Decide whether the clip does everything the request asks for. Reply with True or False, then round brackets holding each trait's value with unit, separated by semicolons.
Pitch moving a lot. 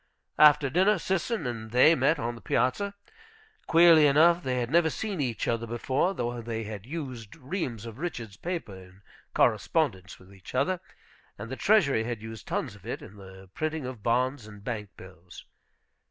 True (6.4 semitones)